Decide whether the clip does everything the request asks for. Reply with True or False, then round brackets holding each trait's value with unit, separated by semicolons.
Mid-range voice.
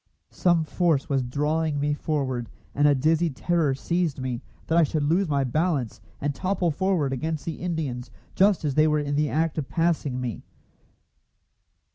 True (150 Hz)